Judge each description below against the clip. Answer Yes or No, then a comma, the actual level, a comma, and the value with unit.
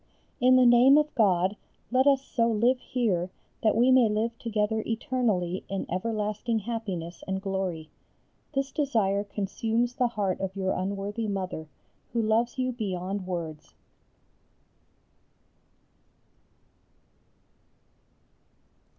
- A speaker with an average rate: No, slow, 110 wpm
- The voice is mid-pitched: No, high, 215 Hz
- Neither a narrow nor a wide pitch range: Yes, average, 3.9 semitones